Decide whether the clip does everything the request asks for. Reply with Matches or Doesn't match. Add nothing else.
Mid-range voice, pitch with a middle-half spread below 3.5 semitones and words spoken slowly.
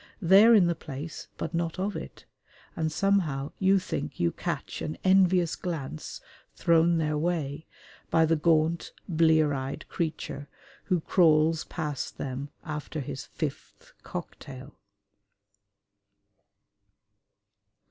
Matches